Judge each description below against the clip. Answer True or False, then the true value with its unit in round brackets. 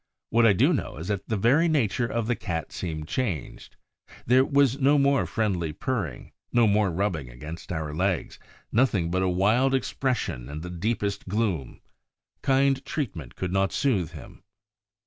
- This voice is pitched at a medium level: False (100 Hz)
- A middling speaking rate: True (165 wpm)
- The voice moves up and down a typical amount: False (7.0 semitones)